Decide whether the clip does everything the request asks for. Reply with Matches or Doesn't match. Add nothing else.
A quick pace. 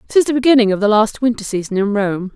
Matches